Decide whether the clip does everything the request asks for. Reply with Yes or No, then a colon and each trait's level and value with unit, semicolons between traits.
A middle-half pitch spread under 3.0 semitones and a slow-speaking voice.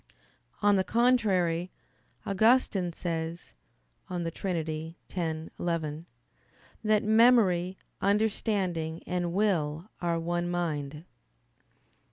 No: average, 3.7 semitones; slow, 85 wpm